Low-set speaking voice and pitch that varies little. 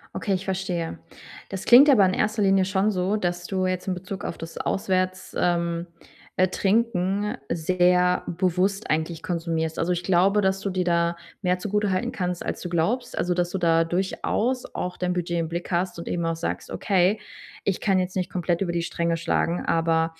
No: medium, 180 Hz; narrow, 2.1 semitones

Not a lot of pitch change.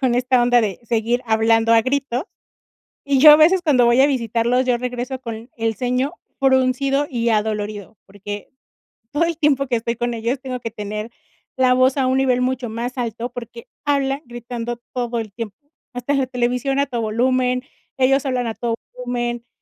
Yes: narrow, 2.2 semitones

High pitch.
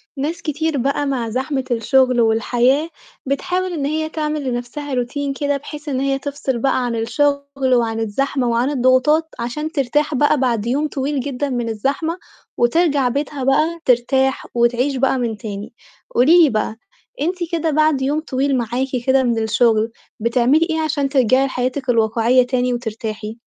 Yes: very high, 265 Hz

